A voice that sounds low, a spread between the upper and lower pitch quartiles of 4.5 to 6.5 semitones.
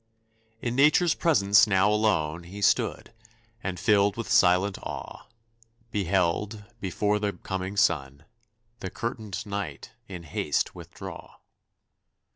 No: low, 100 Hz; average, 2.8 semitones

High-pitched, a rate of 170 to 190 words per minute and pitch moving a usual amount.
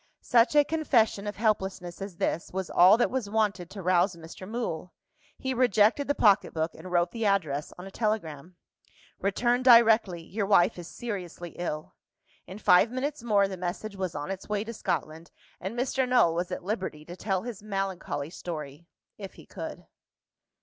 Yes: high, 195 Hz; average, 175 wpm; average, 4.2 semitones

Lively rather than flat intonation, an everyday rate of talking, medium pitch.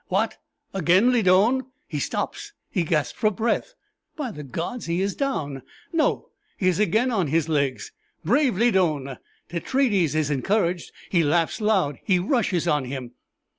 Yes: wide, 6.3 semitones; average, 150 wpm; medium, 180 Hz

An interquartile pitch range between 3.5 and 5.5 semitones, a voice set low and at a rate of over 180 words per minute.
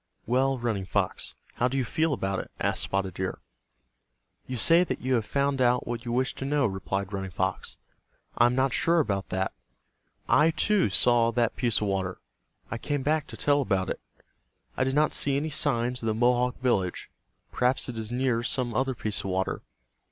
Yes: average, 4.4 semitones; low, 120 Hz; average, 195 wpm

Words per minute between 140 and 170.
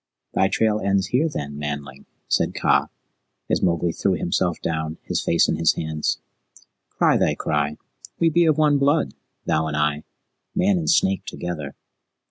Yes: average, 160 wpm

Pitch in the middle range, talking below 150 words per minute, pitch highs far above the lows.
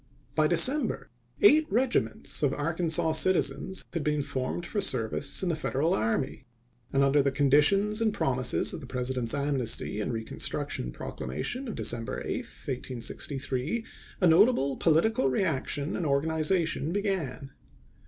Yes: medium, 150 Hz; average, 140 wpm; wide, 6.0 semitones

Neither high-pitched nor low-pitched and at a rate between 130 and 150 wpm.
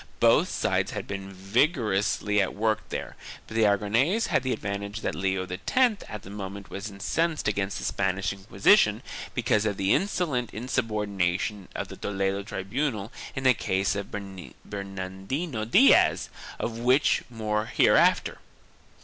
No: low, 105 Hz; average, 140 wpm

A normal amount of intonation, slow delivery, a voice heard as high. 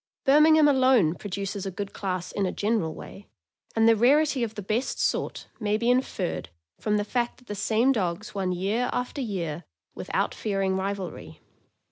No: average, 4.4 semitones; average, 170 wpm; high, 210 Hz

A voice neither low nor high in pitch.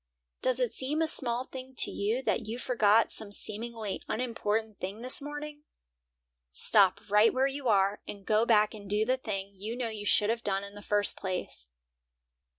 No: high, 220 Hz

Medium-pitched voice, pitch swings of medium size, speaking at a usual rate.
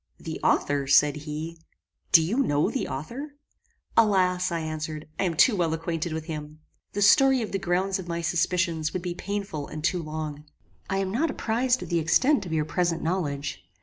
Yes: medium, 170 Hz; average, 3.9 semitones; average, 190 wpm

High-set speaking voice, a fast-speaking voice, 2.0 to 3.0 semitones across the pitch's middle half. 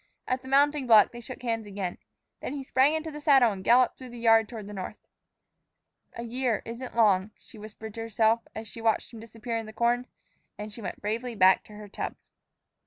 Yes: high, 230 Hz; fast, 215 wpm; average, 2.7 semitones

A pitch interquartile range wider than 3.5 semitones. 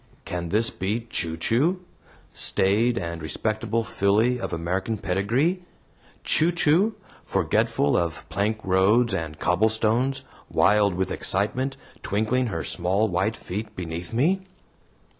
Yes: average, 4.5 semitones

